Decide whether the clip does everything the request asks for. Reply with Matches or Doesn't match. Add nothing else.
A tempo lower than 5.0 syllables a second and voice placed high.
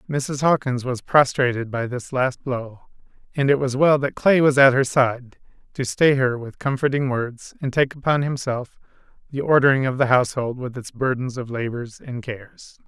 Doesn't match